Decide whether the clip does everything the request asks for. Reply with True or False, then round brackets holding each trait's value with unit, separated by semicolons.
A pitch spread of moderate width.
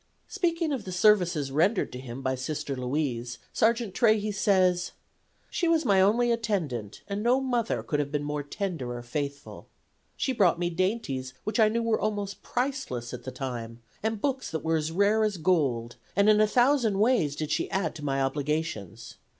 False (8.0 semitones)